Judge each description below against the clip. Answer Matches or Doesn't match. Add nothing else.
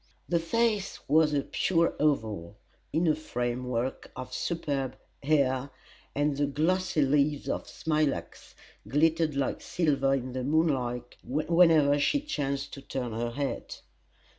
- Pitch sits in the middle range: Matches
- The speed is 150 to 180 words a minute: Doesn't match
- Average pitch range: Matches